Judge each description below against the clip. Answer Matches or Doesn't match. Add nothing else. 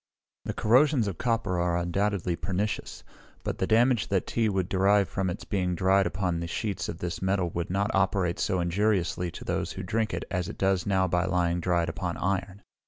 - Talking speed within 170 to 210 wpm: Matches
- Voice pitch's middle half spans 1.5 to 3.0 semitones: Matches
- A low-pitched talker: Matches